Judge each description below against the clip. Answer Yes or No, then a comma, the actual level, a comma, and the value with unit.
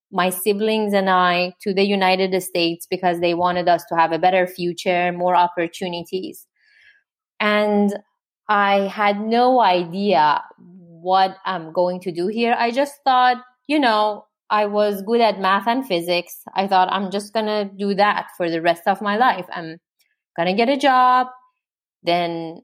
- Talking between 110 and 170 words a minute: Yes, average, 165 wpm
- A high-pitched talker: Yes, high, 195 Hz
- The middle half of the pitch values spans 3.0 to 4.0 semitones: Yes, average, 3.7 semitones